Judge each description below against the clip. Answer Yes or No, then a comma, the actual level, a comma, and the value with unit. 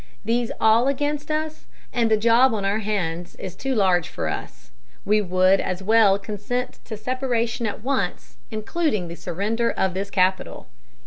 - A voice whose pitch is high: Yes, high, 215 Hz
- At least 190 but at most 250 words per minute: No, average, 165 wpm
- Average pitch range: Yes, average, 4.1 semitones